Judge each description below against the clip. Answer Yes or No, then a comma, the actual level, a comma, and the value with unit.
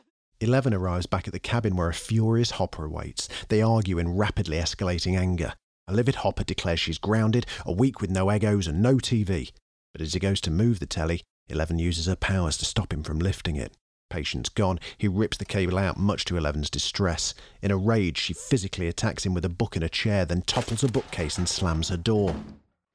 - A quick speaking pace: Yes, fast, 210 wpm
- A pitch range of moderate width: Yes, average, 4.2 semitones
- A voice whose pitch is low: Yes, very low, 95 Hz